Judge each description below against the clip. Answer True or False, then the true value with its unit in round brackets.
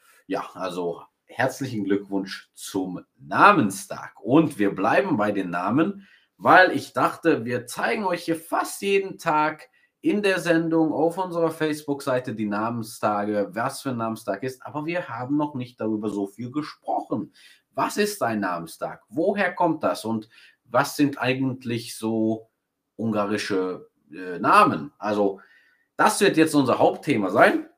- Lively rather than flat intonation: True (7.1 semitones)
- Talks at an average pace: True (145 wpm)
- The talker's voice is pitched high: False (125 Hz)